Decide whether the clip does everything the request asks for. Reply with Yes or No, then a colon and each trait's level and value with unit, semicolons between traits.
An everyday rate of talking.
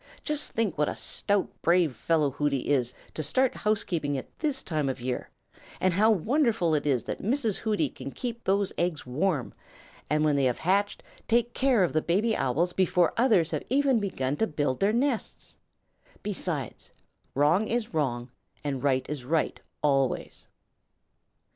Yes: average, 165 wpm